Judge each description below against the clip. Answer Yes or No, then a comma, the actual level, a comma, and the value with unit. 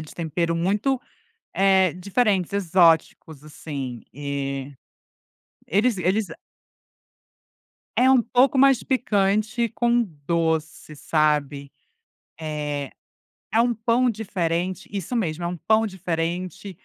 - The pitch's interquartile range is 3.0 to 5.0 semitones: No, wide, 5.5 semitones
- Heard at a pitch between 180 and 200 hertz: Yes, medium, 185 Hz